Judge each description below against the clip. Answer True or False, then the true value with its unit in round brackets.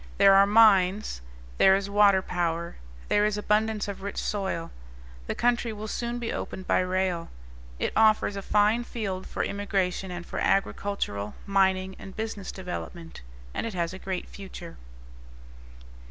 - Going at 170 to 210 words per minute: False (155 wpm)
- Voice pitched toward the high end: True (195 Hz)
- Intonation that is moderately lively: False (2.2 semitones)